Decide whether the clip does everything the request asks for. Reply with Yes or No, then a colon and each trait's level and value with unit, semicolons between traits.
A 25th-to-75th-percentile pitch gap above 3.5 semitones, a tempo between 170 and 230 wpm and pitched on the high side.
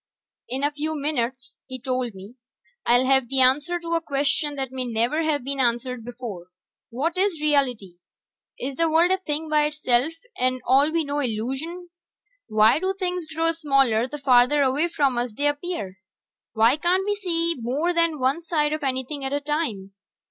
Yes: average, 4.3 semitones; average, 180 wpm; very high, 280 Hz